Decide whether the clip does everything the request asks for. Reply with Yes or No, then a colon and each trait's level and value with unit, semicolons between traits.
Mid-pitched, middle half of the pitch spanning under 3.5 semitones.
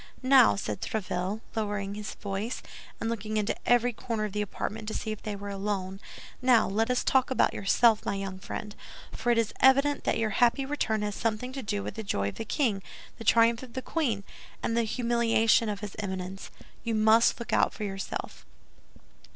No: high, 220 Hz; average, 2.7 semitones